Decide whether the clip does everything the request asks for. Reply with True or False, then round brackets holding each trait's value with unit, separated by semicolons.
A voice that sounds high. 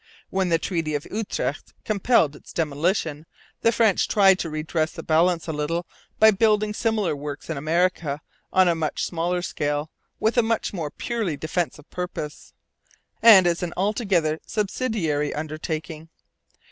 False (170 Hz)